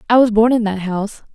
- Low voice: No, high, 215 Hz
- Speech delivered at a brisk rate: Yes, fast, 265 wpm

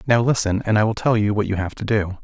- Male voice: Yes, male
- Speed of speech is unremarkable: No, fast, 320 wpm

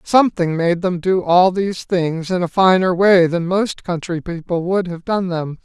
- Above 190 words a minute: Yes, average, 200 wpm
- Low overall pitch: No, medium, 180 Hz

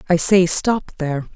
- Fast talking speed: No, average, 175 wpm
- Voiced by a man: No, female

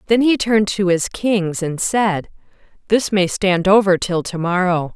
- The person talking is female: Yes, female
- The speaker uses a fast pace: No, average, 180 wpm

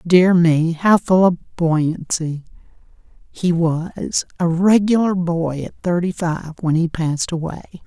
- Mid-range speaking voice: Yes, medium, 170 Hz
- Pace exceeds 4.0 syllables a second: No, 3.6 syllables/s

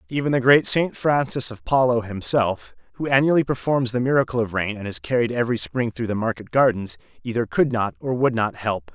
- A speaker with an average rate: No, fast, 210 wpm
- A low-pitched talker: Yes, low, 120 Hz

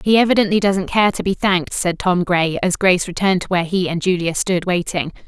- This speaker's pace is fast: Yes, fast, 225 wpm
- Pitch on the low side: No, medium, 185 Hz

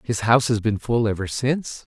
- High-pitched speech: No, low, 115 Hz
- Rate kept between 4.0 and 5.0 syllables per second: No, 5.6 syllables/s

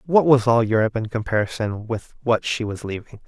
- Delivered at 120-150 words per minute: No, average, 200 wpm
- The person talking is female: No, male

